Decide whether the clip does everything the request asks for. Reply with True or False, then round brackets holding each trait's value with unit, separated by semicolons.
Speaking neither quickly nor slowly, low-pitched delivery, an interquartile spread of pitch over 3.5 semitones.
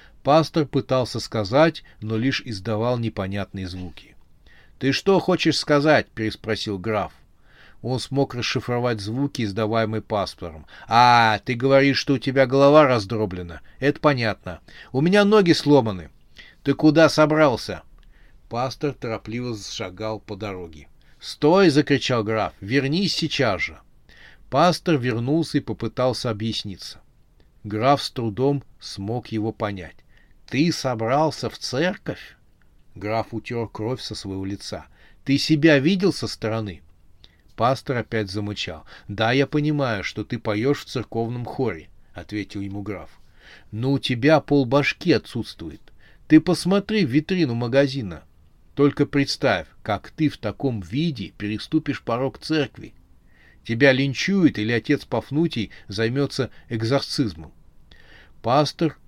True (120 wpm; 115 Hz; 5.4 semitones)